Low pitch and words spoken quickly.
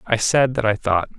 Yes: low, 115 Hz; fast, 255 wpm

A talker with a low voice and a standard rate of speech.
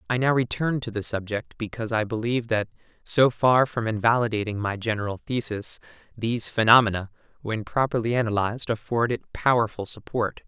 Yes: low, 115 Hz; average, 150 wpm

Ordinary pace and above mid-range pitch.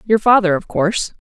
Yes: average, 195 wpm; high, 195 Hz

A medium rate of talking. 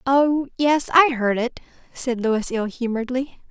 Yes: average, 155 wpm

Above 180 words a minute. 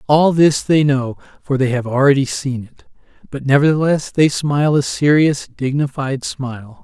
No: average, 160 wpm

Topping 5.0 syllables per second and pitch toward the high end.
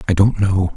No: 5.3 syllables/s; very low, 95 Hz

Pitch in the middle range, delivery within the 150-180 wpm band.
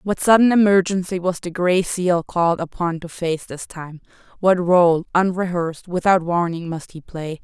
Yes: medium, 175 Hz; average, 160 wpm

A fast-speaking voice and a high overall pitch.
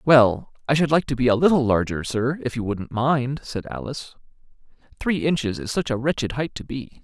No: fast, 215 wpm; low, 130 Hz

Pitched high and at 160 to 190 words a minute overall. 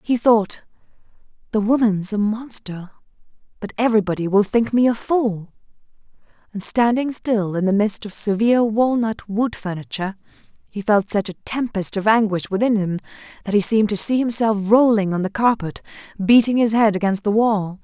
Yes: high, 215 Hz; average, 165 wpm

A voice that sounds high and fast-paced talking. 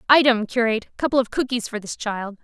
No: high, 235 Hz; average, 195 wpm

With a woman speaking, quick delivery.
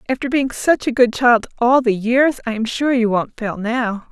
Yes: female; fast, 235 wpm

